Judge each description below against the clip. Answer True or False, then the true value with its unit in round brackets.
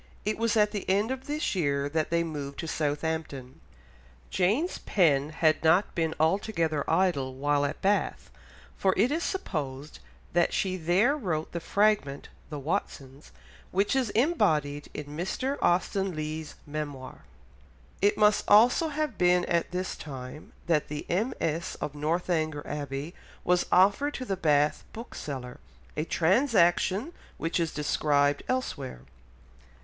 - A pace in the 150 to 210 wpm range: False (140 wpm)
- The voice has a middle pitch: True (170 Hz)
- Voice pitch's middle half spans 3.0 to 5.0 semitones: False (5.5 semitones)